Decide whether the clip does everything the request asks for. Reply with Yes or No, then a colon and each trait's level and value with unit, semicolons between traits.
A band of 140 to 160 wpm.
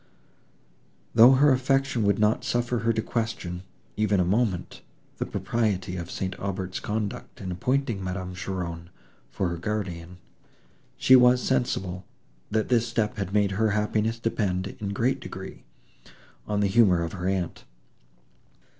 Yes: average, 145 wpm